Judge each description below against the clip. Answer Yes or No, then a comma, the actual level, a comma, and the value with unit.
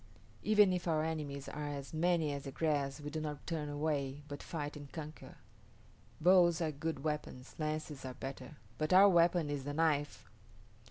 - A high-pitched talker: No, medium, 150 Hz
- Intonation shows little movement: Yes, narrow, 2.2 semitones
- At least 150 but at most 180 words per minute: Yes, average, 175 wpm